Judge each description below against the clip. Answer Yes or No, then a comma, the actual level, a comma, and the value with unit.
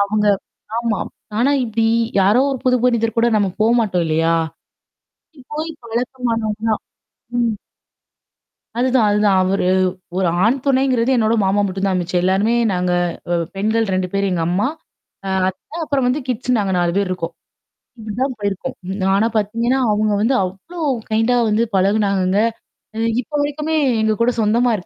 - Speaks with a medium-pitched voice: No, high, 220 Hz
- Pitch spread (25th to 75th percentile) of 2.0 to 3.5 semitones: No, average, 4.0 semitones